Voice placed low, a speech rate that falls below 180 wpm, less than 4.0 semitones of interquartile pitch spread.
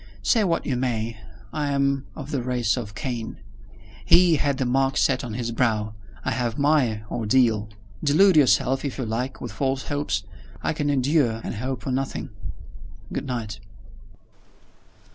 Yes: low, 130 Hz; average, 160 wpm; average, 3.6 semitones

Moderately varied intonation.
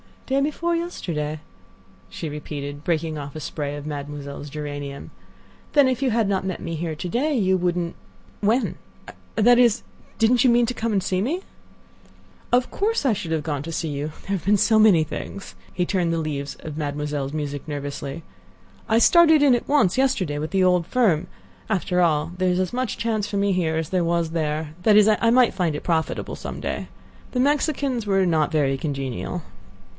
No: wide, 7.1 semitones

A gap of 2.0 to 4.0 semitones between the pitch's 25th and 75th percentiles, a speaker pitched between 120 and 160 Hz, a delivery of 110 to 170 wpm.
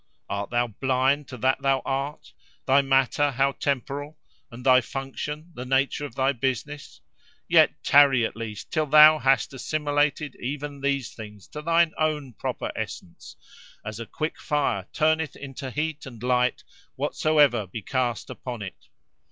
Yes: average, 2.9 semitones; low, 135 Hz; average, 150 wpm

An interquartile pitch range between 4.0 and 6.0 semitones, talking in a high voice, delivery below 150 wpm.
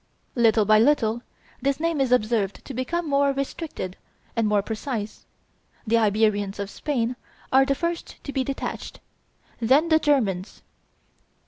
Yes: average, 4.6 semitones; high, 245 Hz; average, 140 wpm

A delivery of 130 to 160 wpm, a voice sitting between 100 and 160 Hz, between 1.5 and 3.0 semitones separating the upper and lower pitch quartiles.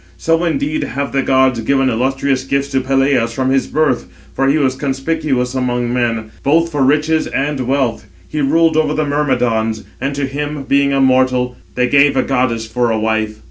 No: average, 190 wpm; low, 135 Hz; narrow, 2.5 semitones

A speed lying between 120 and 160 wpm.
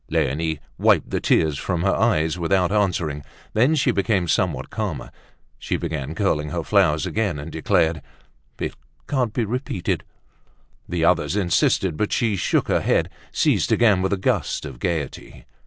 Yes: average, 155 wpm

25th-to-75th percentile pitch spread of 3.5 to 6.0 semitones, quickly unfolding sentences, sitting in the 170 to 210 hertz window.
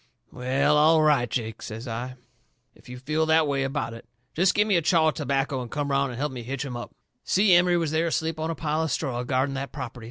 No: average, 3.9 semitones; fast, 250 wpm; medium, 140 Hz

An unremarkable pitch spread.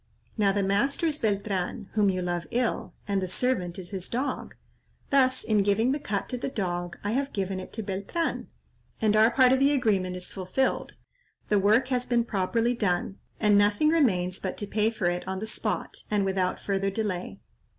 Yes: average, 4.2 semitones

